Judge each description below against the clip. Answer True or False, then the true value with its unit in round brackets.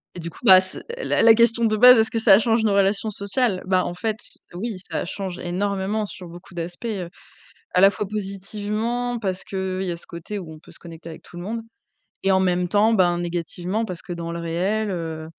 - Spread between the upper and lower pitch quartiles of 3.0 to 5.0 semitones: True (3.6 semitones)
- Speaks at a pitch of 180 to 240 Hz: True (190 Hz)